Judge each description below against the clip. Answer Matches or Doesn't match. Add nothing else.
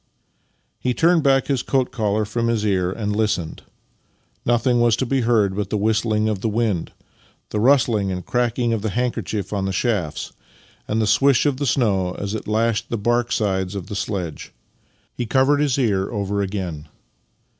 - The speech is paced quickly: Doesn't match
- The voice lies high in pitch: Doesn't match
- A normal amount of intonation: Matches